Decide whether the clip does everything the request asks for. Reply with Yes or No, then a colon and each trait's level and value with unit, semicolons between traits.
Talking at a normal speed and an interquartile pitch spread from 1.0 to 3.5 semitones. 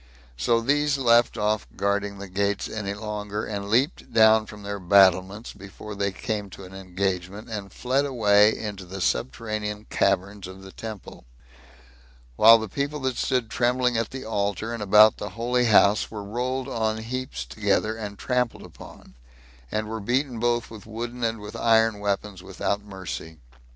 Yes: average, 165 wpm; narrow, 2.6 semitones